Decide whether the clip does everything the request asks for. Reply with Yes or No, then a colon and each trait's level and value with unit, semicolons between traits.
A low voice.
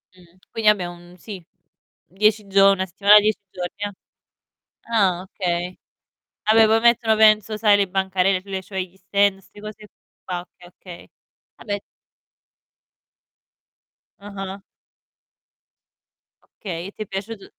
No: high, 195 Hz